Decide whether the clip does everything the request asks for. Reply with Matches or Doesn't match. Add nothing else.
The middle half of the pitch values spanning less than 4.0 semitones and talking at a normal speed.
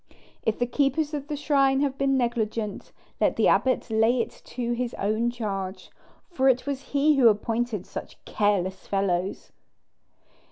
Doesn't match